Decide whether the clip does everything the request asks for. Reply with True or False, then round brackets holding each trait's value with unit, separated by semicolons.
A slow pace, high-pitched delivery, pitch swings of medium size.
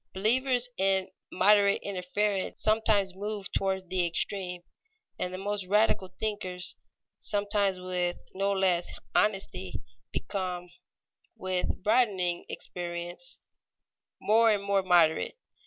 False (105 wpm; 195 Hz; 2.3 semitones)